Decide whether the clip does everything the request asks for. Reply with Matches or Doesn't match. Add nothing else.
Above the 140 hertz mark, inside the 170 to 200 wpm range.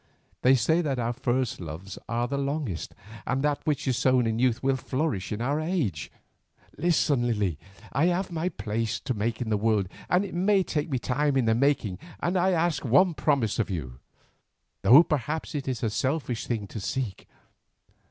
Doesn't match